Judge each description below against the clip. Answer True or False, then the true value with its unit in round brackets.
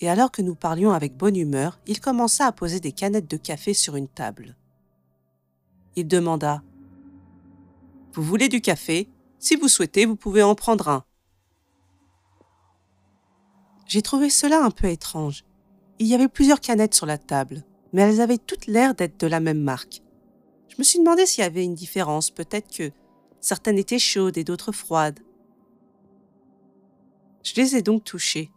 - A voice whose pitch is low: False (175 Hz)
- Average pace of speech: True (165 wpm)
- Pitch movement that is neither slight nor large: False (8.1 semitones)